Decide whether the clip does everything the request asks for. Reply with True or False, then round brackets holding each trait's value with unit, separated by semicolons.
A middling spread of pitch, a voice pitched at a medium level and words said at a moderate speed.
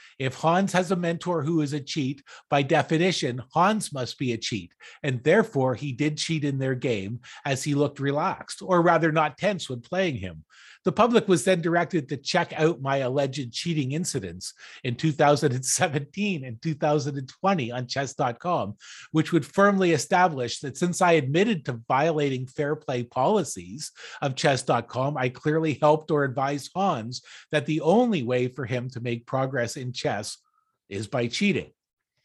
True (4.6 semitones; 150 Hz; 165 wpm)